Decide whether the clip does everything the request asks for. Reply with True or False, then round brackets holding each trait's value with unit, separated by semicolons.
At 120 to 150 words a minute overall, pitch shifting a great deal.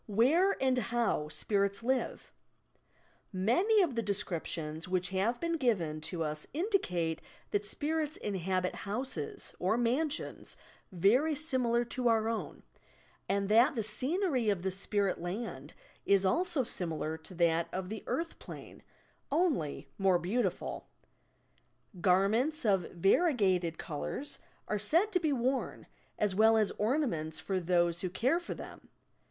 True (145 wpm; 6.3 semitones)